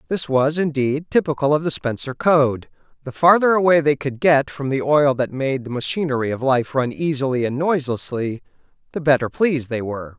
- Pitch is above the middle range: No, medium, 140 Hz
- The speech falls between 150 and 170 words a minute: No, average, 185 wpm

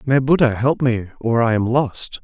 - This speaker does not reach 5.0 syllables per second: Yes, 4.5 syllables/s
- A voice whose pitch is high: No, low, 120 Hz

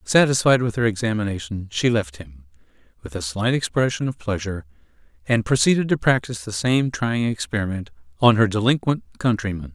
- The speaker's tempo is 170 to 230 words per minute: No, average, 155 wpm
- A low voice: Yes, low, 105 Hz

